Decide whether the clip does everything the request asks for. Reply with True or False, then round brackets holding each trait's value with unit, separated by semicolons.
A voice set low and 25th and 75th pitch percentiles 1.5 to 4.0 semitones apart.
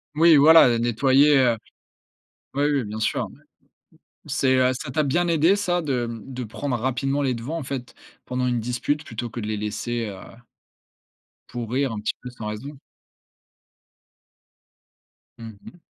True (130 Hz; 3.7 semitones)